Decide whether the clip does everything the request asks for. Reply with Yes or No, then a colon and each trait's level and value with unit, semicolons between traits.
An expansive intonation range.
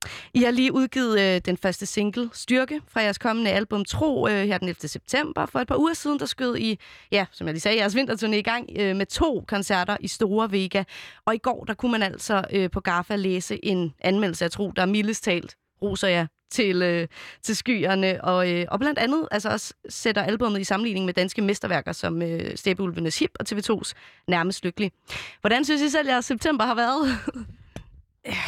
No: average, 4.3 semitones